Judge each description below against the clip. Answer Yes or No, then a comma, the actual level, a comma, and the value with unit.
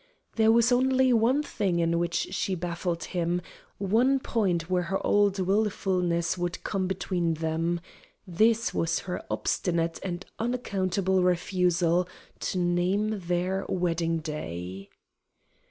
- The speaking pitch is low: No, medium, 180 Hz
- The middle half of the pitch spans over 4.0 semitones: No, average, 3.0 semitones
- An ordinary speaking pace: No, slow, 120 wpm